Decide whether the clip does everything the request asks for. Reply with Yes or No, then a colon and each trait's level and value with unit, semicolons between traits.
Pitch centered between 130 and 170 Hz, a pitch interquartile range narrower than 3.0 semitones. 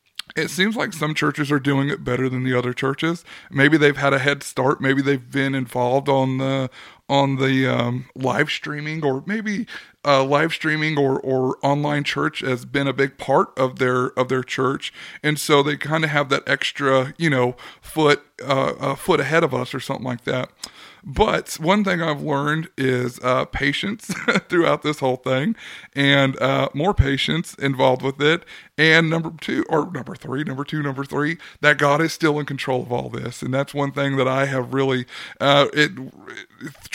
Yes: medium, 140 Hz; narrow, 2.4 semitones